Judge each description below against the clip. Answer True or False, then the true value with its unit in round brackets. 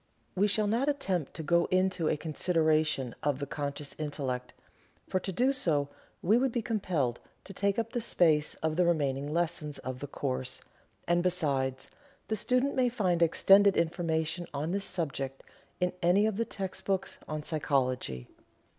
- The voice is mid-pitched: True (170 Hz)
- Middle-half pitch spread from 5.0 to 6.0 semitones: True (5.3 semitones)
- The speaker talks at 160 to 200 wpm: True (165 wpm)